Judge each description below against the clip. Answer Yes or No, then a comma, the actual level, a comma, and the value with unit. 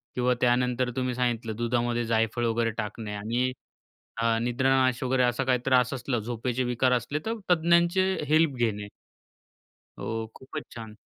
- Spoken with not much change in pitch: Yes, narrow, 2.0 semitones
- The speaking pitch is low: Yes, low, 125 Hz